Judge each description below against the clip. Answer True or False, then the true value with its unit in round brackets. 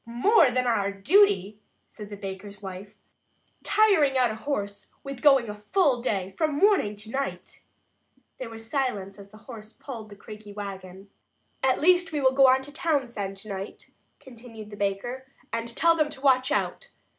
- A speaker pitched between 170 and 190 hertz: False (235 Hz)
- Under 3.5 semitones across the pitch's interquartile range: False (5.3 semitones)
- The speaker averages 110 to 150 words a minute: False (170 wpm)